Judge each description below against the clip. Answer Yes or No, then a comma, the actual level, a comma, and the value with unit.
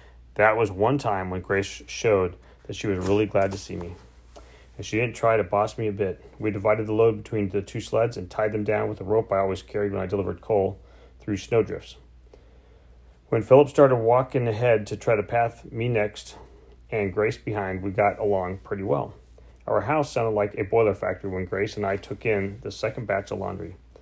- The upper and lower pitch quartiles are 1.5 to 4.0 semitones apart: Yes, average, 3.0 semitones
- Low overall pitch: Yes, low, 105 Hz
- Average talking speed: No, fast, 210 wpm